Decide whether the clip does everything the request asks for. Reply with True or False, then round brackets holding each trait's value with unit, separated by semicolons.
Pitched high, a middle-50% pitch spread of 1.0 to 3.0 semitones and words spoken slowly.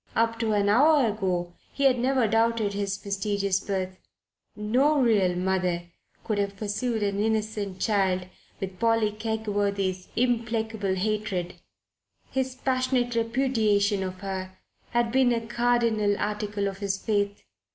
True (210 Hz; 2.7 semitones; 130 wpm)